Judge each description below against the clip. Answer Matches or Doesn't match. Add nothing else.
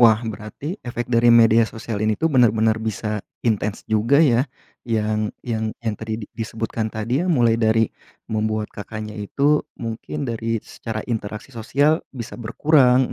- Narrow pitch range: Matches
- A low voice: Matches